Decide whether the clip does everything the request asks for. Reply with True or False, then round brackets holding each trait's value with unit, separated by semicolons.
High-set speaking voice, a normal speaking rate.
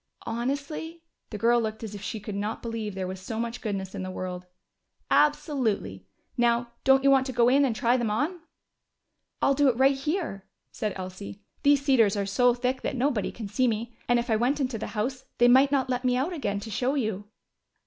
False (240 Hz; 215 wpm)